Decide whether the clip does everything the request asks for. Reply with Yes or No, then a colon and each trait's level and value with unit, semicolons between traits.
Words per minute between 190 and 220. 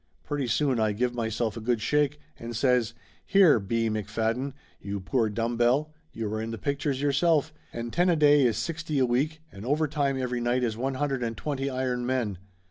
Yes: average, 200 wpm